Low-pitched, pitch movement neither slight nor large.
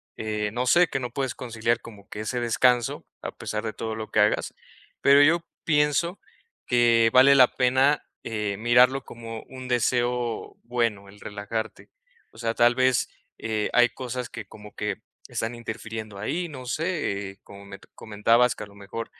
Yes: low, 115 Hz; average, 3.0 semitones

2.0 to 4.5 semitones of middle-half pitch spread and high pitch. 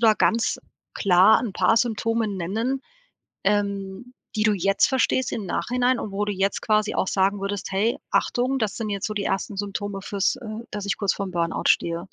Yes: narrow, 2.5 semitones; high, 205 Hz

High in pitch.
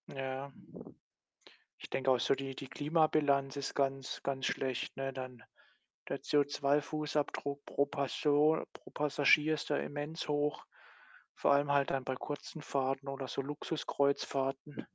No: medium, 140 Hz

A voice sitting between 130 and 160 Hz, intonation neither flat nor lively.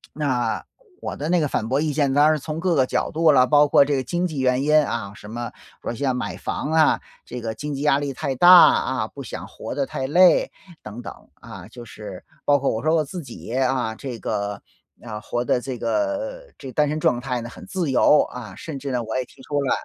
Yes: low, 135 Hz; average, 3.8 semitones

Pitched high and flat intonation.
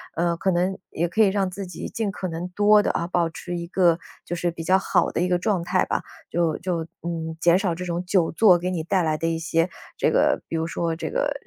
No: medium, 175 Hz; narrow, 2.1 semitones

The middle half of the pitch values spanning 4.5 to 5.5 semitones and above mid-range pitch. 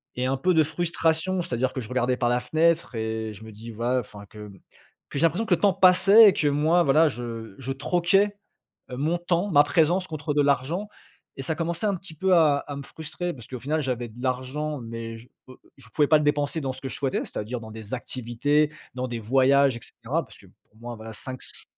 No: average, 5.2 semitones; medium, 140 Hz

